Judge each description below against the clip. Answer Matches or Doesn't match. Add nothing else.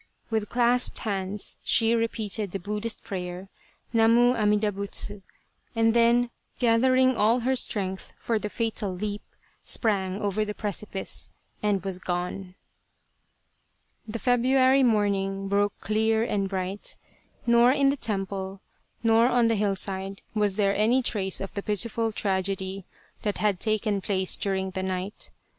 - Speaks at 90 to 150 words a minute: Matches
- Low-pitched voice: Doesn't match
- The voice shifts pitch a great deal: Doesn't match